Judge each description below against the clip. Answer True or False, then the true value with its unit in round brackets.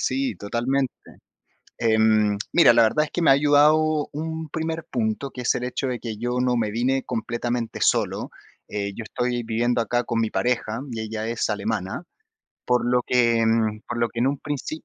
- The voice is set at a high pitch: False (120 Hz)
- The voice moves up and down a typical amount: True (3.5 semitones)